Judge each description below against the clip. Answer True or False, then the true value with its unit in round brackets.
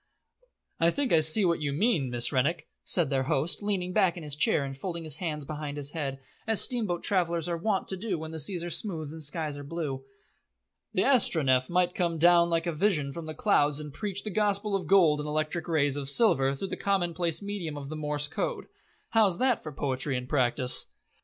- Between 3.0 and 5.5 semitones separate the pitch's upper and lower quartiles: True (4.1 semitones)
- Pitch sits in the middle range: True (165 Hz)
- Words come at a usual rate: False (210 wpm)